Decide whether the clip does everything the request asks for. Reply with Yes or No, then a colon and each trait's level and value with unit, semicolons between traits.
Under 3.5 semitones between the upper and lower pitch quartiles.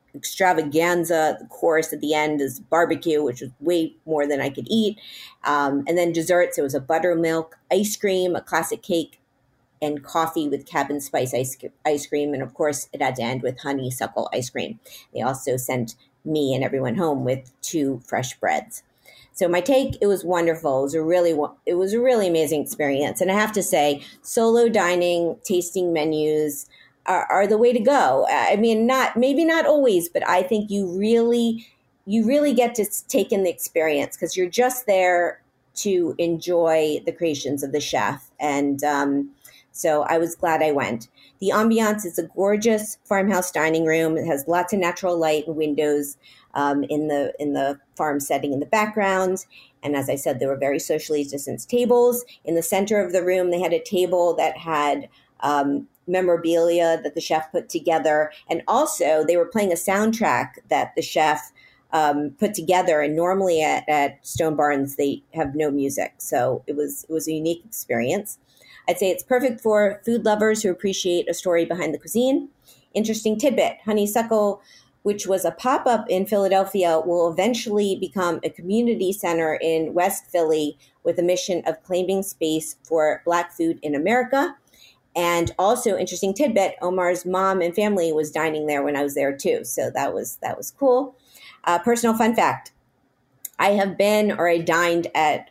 No: average, 4.8 semitones